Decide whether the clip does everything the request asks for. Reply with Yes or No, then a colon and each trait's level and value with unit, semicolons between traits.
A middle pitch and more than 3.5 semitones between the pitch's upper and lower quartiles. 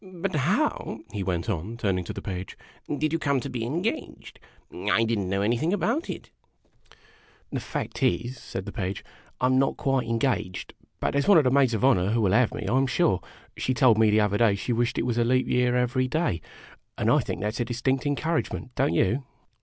No: low, 120 Hz; average, 4.4 semitones